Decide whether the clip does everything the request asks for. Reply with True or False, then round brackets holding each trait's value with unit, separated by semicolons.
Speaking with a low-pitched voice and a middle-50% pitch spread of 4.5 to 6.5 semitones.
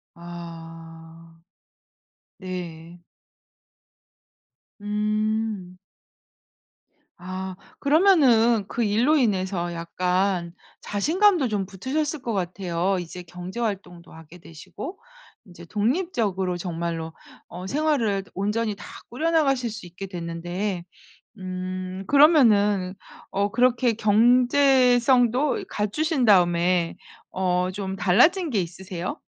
False (195 Hz; 5.3 semitones)